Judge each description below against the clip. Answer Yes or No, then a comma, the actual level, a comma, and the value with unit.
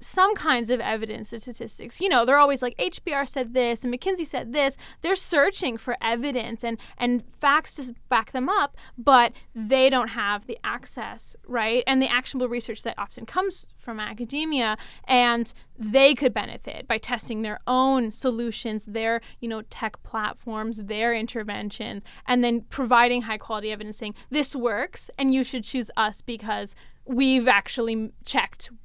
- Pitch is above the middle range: Yes, high, 245 Hz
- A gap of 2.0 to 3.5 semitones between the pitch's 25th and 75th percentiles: Yes, average, 2.7 semitones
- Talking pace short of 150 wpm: No, average, 165 wpm